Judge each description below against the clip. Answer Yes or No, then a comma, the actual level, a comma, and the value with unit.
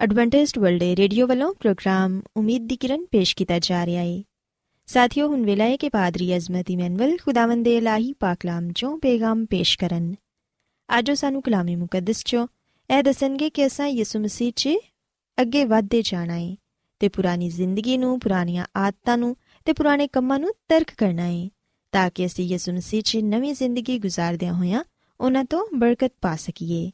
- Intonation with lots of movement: Yes, wide, 6.1 semitones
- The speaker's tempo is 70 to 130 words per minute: No, fast, 165 wpm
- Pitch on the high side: Yes, high, 220 Hz